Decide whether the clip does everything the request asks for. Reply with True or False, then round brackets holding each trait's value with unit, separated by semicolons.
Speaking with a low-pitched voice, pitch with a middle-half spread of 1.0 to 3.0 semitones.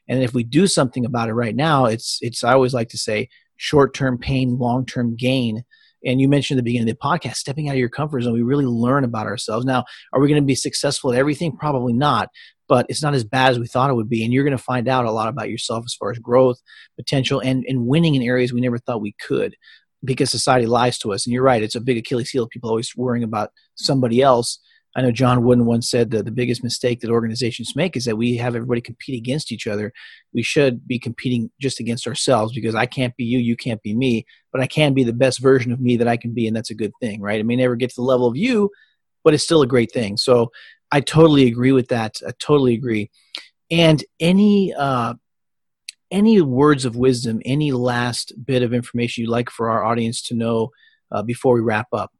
True (125 Hz; 2.4 semitones)